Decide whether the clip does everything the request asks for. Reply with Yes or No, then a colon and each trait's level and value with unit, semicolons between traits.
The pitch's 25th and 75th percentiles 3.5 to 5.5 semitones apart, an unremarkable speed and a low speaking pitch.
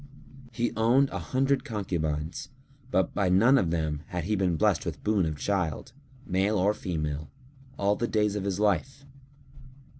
Yes: average, 4.4 semitones; average, 160 wpm; low, 100 Hz